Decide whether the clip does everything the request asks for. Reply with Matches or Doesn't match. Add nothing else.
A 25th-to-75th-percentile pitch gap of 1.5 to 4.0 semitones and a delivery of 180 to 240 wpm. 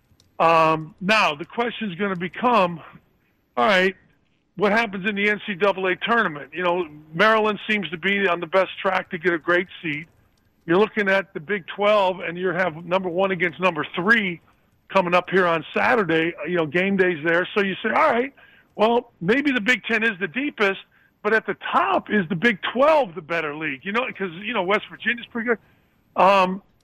Matches